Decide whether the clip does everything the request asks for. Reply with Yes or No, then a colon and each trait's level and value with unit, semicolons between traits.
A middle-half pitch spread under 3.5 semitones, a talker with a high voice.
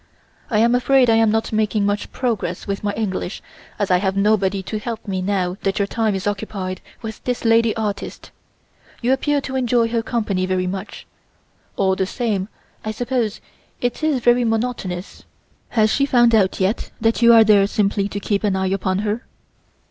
Yes: average, 3.0 semitones; high, 215 Hz